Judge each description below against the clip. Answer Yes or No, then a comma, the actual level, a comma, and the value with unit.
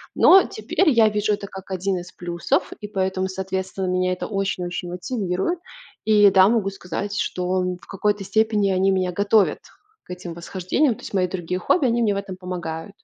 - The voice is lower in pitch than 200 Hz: Yes, high, 190 Hz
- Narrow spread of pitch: Yes, narrow, 2.3 semitones